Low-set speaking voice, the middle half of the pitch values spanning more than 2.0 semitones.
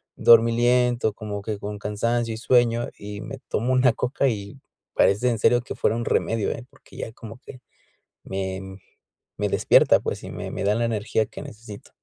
Yes: low, 115 Hz; narrow, 2.6 semitones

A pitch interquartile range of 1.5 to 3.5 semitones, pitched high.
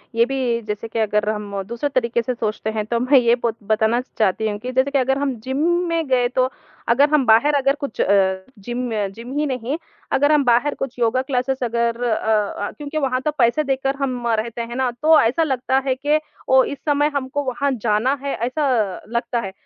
Yes: average, 3.0 semitones; very high, 250 Hz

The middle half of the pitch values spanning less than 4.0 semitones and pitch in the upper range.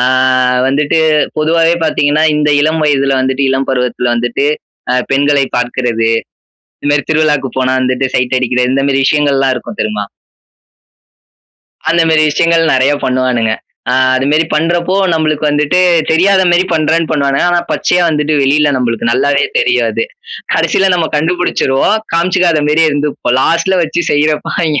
No: average, 3.6 semitones; medium, 145 Hz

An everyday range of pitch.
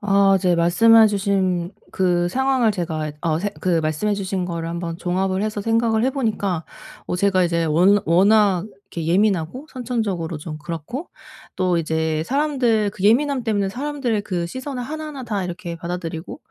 Yes: average, 4.8 semitones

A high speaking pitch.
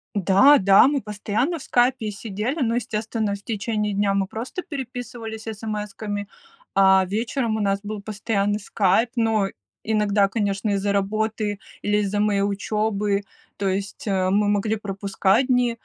Yes: high, 210 Hz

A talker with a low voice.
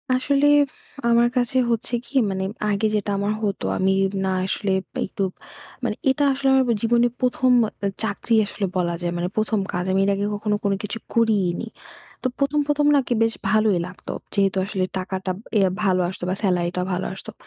No: high, 205 Hz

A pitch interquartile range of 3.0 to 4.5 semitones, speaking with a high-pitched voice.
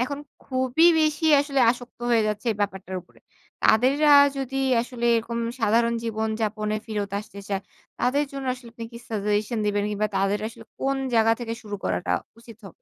Yes: average, 3.4 semitones; high, 230 Hz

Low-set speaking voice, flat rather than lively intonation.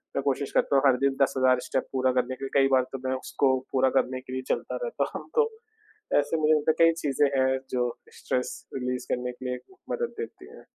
Yes: low, 130 Hz; narrow, 1.9 semitones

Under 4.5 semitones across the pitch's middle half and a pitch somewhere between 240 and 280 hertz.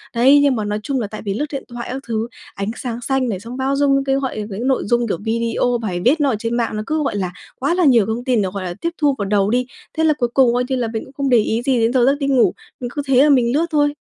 Yes: average, 3.5 semitones; high, 245 Hz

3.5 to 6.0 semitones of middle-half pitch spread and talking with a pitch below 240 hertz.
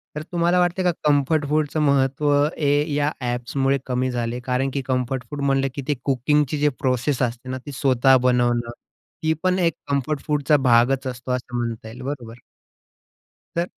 No: average, 3.0 semitones; low, 135 Hz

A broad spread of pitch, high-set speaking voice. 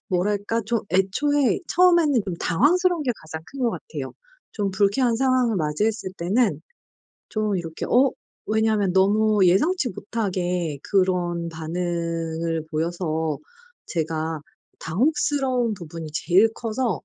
Yes: wide, 6.0 semitones; high, 195 Hz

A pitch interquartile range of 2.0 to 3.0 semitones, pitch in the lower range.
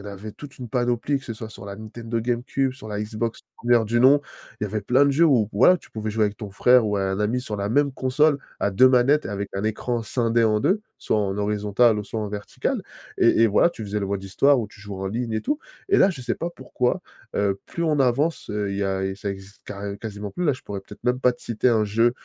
No: average, 3.6 semitones; low, 110 Hz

